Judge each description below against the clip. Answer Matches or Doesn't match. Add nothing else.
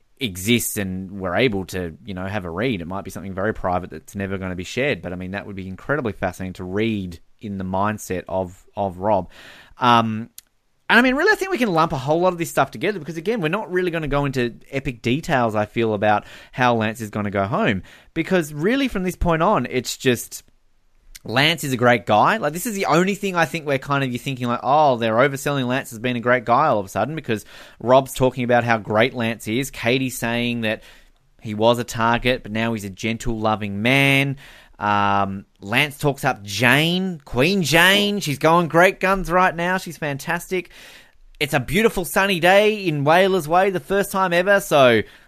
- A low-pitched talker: Matches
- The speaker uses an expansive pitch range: Matches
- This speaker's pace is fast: Matches